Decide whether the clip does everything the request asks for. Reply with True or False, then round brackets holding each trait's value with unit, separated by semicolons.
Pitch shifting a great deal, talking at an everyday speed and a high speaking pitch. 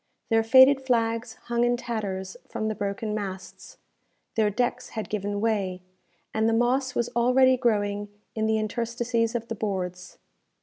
False (2.7 semitones; 155 wpm; 225 Hz)